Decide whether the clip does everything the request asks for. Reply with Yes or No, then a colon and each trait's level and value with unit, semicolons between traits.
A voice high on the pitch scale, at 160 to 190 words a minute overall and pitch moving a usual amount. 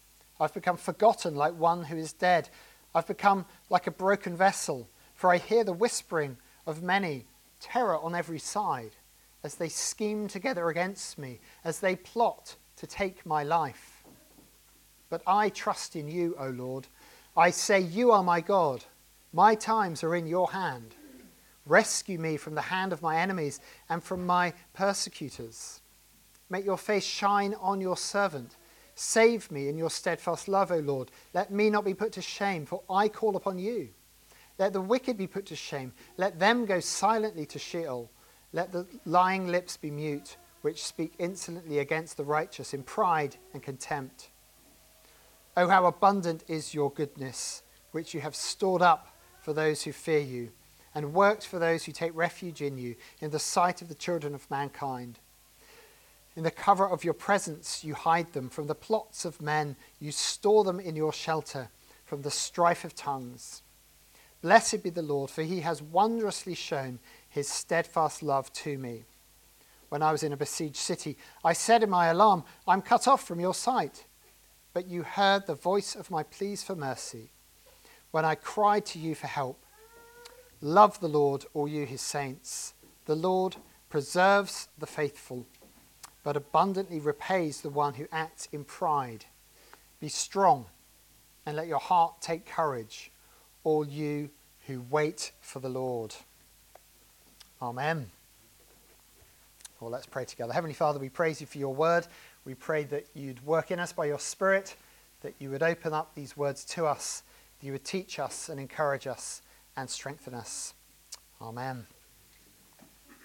No: medium, 165 Hz; average, 165 wpm; average, 4.6 semitones